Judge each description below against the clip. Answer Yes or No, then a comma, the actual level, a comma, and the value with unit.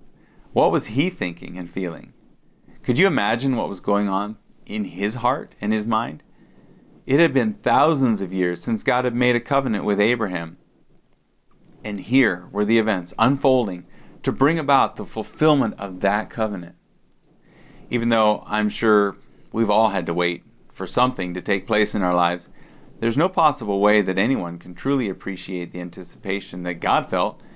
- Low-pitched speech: Yes, low, 105 Hz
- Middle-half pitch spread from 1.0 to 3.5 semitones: No, average, 4.2 semitones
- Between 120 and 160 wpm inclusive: No, average, 170 wpm